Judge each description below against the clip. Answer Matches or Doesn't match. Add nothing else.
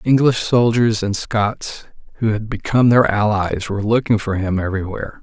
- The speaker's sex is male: Matches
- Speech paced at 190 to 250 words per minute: Doesn't match